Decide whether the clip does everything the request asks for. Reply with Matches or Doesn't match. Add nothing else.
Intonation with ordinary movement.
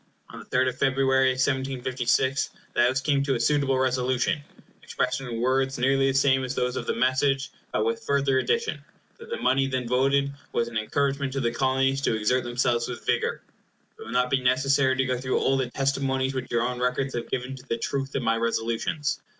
Doesn't match